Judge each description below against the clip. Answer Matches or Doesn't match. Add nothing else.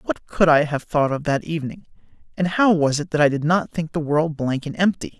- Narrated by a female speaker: Doesn't match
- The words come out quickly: Matches